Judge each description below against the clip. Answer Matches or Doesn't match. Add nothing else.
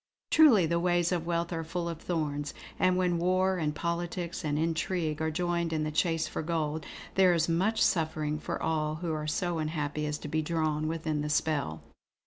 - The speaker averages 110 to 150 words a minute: Doesn't match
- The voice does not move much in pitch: Matches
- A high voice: Doesn't match